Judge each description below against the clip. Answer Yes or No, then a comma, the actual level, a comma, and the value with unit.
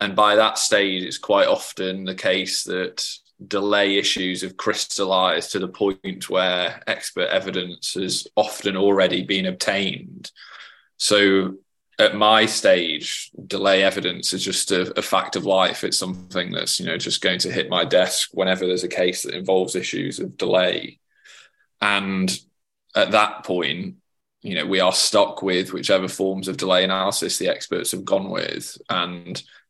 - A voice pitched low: Yes, very low, 95 Hz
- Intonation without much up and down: Yes, narrow, 1.2 semitones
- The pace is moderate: Yes, average, 160 wpm